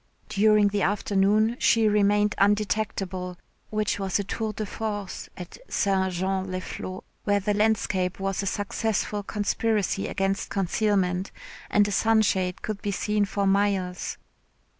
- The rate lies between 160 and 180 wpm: No, average, 140 wpm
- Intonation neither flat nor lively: No, narrow, 1.7 semitones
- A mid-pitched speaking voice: No, high, 200 Hz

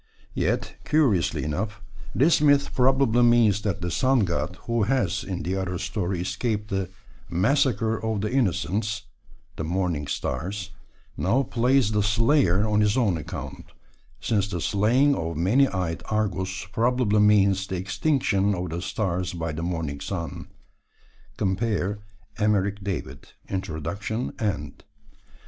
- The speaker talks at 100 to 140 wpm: Yes, slow, 135 wpm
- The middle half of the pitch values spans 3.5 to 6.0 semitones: Yes, average, 3.9 semitones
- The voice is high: No, low, 100 Hz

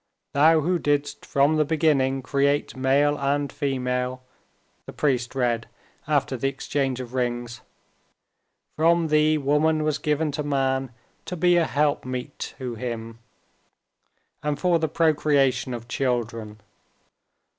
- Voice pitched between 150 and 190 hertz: No, medium, 140 Hz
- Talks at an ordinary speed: No, slow, 125 wpm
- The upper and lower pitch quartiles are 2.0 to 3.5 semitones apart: Yes, average, 3.1 semitones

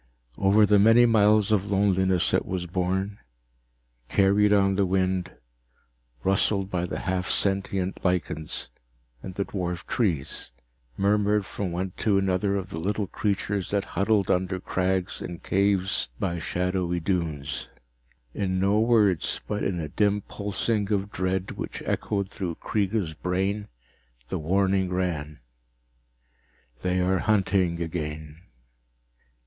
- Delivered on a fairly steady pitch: Yes, narrow, 2.1 semitones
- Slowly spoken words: Yes, slow, 130 wpm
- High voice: No, very low, 95 Hz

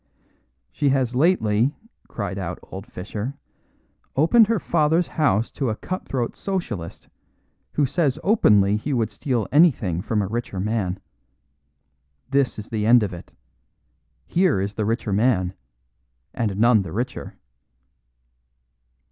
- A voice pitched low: Yes, low, 115 Hz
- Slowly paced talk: Yes, slow, 130 wpm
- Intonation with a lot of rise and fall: Yes, wide, 5.7 semitones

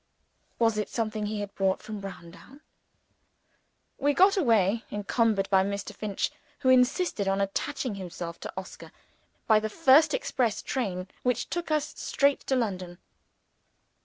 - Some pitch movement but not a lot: Yes, average, 5.0 semitones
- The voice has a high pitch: Yes, high, 215 Hz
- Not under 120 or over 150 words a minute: Yes, average, 140 wpm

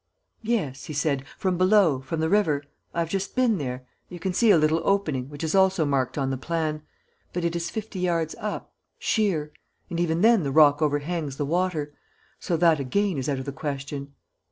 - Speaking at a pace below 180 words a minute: No, fast, 205 wpm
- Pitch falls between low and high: Yes, medium, 160 Hz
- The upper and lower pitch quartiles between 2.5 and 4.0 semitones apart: No, average, 4.5 semitones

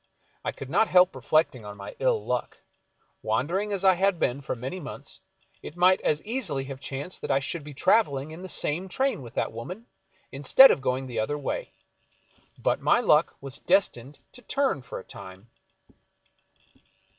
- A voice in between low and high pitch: Yes, medium, 150 Hz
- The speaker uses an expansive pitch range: Yes, wide, 6.1 semitones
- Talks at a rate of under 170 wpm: No, average, 180 wpm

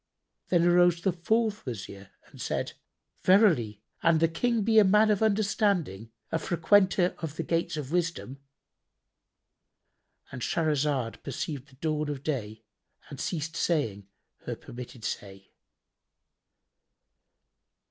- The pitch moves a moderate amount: No, wide, 6.1 semitones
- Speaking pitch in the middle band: Yes, medium, 160 Hz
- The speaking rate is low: Yes, slow, 115 wpm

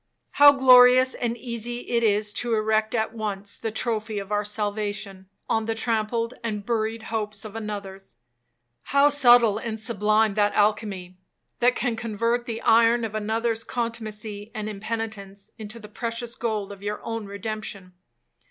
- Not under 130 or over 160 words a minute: Yes, average, 150 wpm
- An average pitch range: No, narrow, 1.9 semitones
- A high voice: Yes, high, 220 Hz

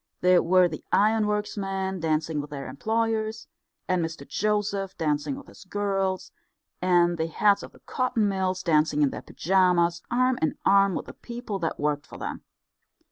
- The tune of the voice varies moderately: Yes, average, 4.2 semitones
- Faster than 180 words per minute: No, average, 170 wpm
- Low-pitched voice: No, medium, 185 Hz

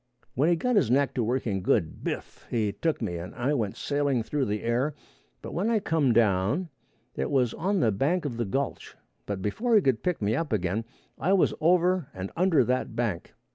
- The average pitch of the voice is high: No, low, 130 Hz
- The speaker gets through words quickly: Yes, fast, 210 wpm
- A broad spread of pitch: Yes, wide, 7.3 semitones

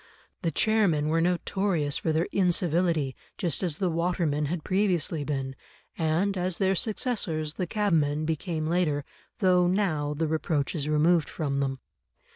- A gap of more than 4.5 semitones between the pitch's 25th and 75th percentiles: No, average, 3.3 semitones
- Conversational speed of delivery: Yes, average, 145 wpm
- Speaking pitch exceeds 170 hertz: No, medium, 165 Hz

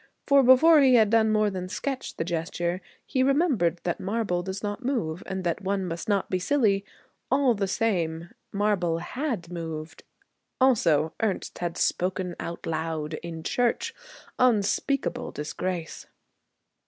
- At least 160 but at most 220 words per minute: No, average, 140 wpm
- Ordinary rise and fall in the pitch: No, wide, 5.7 semitones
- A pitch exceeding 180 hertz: Yes, high, 190 Hz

